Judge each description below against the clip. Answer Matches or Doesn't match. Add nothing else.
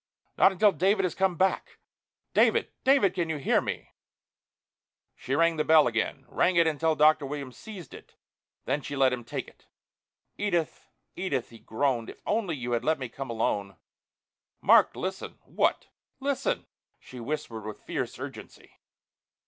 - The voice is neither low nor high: Matches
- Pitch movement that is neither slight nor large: Doesn't match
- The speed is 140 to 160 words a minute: Matches